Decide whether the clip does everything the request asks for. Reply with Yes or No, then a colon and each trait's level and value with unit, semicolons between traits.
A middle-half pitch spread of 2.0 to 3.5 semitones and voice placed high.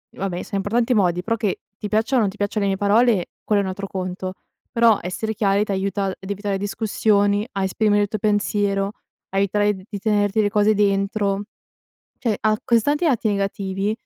No: narrow, 1.6 semitones; high, 205 Hz